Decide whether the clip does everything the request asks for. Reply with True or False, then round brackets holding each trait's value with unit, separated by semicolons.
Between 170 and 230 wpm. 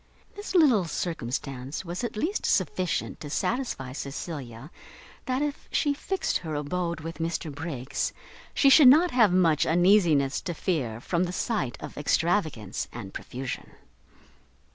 False (140 wpm)